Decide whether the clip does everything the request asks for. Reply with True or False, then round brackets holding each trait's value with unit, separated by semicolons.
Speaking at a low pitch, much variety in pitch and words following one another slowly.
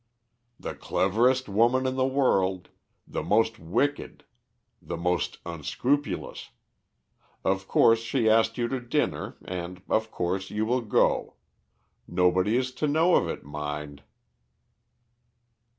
True (110 Hz; 5.9 semitones; 120 wpm)